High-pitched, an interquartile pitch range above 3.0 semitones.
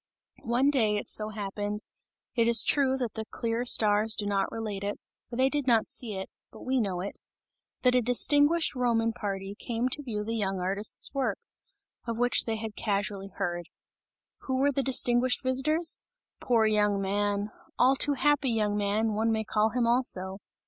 Yes: high, 225 Hz; average, 3.6 semitones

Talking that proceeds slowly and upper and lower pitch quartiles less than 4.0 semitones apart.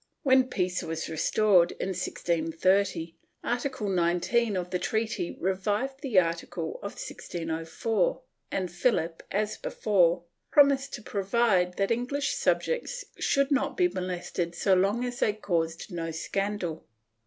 No: slow, 130 wpm; wide, 5.5 semitones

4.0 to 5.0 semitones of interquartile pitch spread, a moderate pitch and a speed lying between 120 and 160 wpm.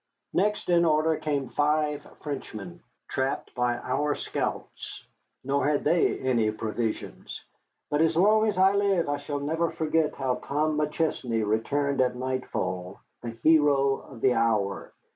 Yes: average, 4.3 semitones; medium, 145 Hz; average, 145 wpm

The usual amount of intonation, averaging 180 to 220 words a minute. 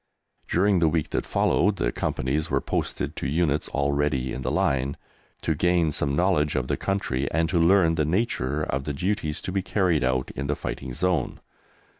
Yes: average, 4.1 semitones; average, 190 wpm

